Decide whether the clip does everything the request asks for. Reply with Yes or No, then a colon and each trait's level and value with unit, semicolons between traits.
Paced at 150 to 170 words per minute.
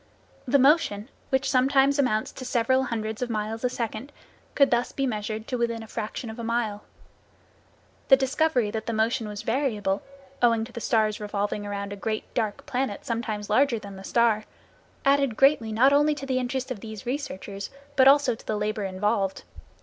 No: average, 185 wpm